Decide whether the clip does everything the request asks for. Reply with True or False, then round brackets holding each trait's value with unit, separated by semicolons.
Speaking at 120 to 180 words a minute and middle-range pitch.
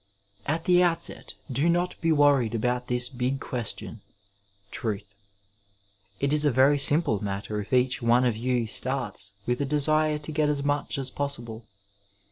False (165 wpm; 130 Hz)